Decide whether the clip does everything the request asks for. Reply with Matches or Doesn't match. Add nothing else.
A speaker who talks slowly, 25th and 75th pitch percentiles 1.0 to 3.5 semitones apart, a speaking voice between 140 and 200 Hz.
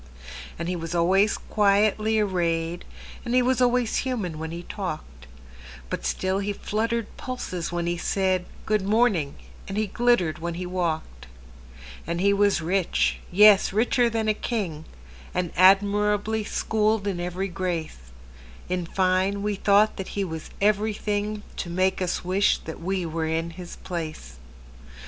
Doesn't match